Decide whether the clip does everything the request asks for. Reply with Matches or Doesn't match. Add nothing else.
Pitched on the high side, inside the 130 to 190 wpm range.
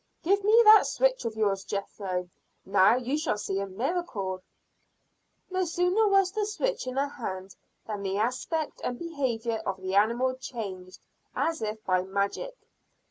Matches